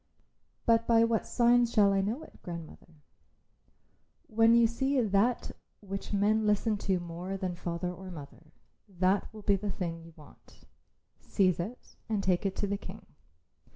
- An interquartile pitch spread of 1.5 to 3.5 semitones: No, average, 3.9 semitones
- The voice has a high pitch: Yes, high, 200 Hz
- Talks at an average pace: Yes, average, 165 wpm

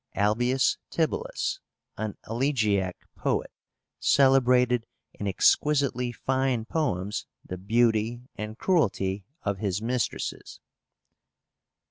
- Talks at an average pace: No, slow, 85 wpm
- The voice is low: Yes, low, 115 Hz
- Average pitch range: Yes, average, 4.2 semitones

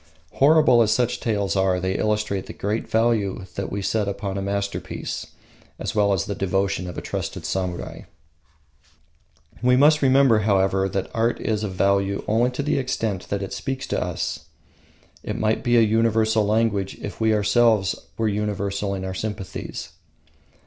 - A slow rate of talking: No, average, 165 wpm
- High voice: No, low, 105 Hz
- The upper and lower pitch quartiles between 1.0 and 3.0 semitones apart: Yes, narrow, 2.6 semitones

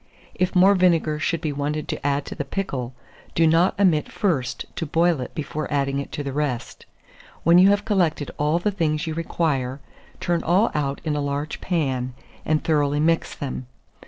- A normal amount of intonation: Yes, average, 3.3 semitones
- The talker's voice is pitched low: No, medium, 155 Hz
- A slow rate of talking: No, average, 190 wpm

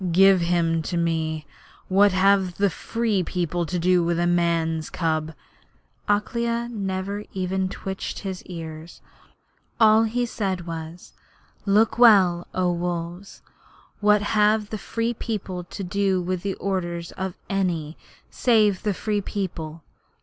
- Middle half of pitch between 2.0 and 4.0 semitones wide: Yes, average, 3.1 semitones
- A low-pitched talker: No, medium, 185 Hz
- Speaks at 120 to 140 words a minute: Yes, slow, 135 wpm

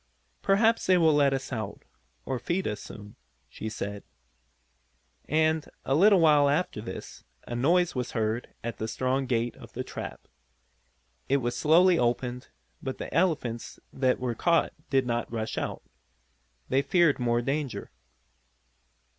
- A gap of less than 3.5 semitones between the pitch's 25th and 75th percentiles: No, average, 5.1 semitones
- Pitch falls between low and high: No, low, 130 Hz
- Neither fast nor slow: Yes, average, 145 wpm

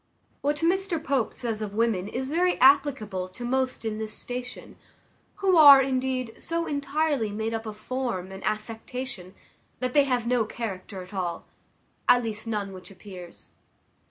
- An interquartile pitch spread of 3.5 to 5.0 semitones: Yes, average, 4.4 semitones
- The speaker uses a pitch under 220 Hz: No, high, 240 Hz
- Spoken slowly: No, average, 155 wpm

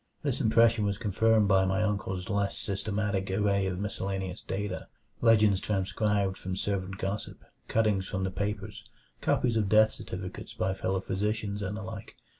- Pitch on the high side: No, low, 100 Hz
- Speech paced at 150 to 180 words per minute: Yes, average, 155 wpm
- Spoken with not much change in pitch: Yes, narrow, 2.0 semitones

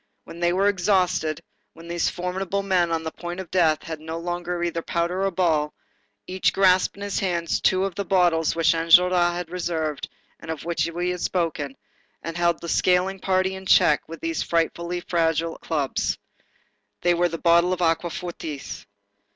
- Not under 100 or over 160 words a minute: No, average, 175 wpm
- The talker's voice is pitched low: No, medium, 175 Hz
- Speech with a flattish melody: Yes, narrow, 1.8 semitones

